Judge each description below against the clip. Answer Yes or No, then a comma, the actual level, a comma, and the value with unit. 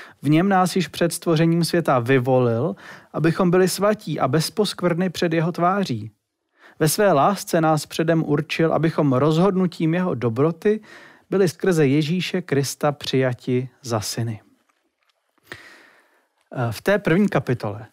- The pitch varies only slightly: No, average, 5.1 semitones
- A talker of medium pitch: Yes, medium, 160 Hz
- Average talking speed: Yes, average, 125 wpm